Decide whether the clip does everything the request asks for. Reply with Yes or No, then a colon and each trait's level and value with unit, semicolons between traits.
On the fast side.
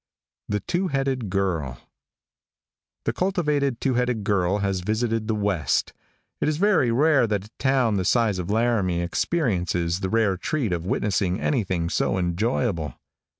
No: average, 150 wpm